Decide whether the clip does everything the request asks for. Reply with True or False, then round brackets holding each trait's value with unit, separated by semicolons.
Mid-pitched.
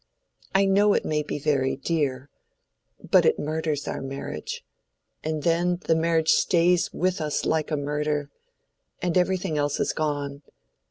True (155 Hz)